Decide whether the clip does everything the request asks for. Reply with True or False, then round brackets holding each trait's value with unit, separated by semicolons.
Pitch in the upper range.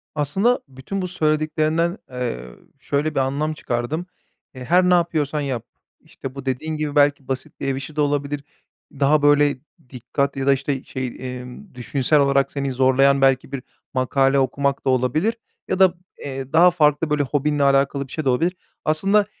False (140 Hz)